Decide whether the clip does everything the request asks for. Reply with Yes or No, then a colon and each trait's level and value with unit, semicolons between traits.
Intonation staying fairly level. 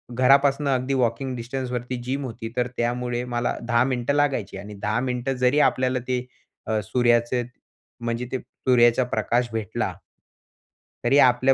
Yes: narrow, 1.7 semitones